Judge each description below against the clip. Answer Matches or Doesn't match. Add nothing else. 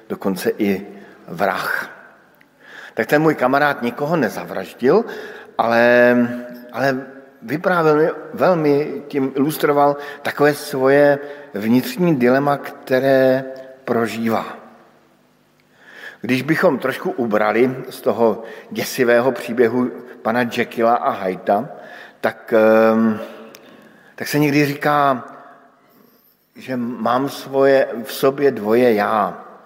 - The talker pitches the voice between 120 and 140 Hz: Matches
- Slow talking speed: Matches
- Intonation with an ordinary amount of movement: Matches